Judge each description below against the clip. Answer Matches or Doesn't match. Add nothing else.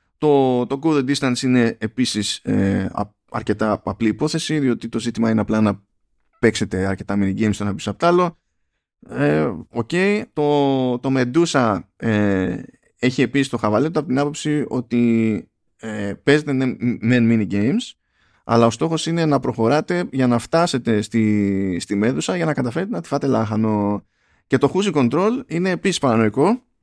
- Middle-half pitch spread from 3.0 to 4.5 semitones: Doesn't match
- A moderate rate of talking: Matches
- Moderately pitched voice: Doesn't match